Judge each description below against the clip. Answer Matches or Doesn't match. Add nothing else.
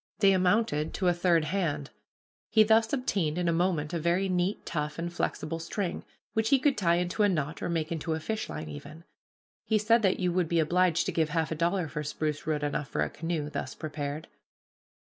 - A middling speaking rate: Doesn't match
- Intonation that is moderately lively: Matches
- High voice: Doesn't match